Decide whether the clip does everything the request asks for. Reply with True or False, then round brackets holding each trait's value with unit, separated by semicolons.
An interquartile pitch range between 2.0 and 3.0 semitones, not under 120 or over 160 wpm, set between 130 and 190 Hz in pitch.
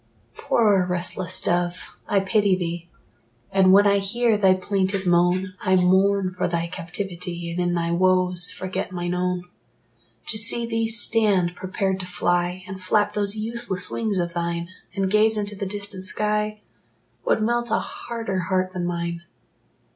True (2.6 semitones; 155 wpm; 185 Hz)